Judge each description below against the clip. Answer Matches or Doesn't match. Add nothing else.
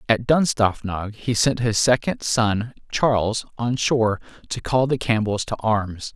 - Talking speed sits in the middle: Matches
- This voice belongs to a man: Matches